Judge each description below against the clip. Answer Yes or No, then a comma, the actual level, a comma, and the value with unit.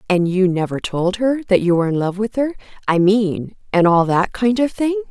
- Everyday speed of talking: No, fast, 225 wpm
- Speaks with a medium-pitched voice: No, high, 200 Hz